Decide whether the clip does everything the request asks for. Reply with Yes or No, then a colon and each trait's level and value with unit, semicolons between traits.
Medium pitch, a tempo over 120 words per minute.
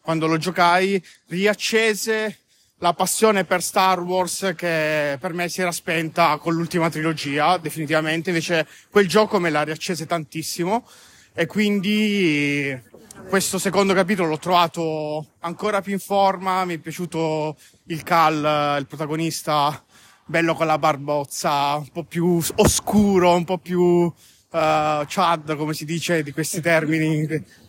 Yes: medium, 170 Hz; average, 135 wpm